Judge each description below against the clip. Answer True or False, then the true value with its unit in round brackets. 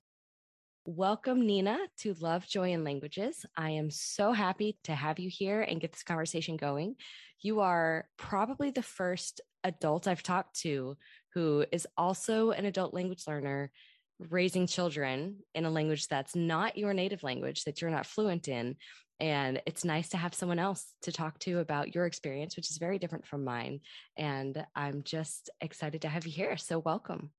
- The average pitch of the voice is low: False (170 Hz)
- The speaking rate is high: False (175 wpm)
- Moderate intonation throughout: True (3.7 semitones)